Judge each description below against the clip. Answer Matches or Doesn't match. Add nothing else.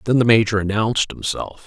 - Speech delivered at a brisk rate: Doesn't match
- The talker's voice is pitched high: Doesn't match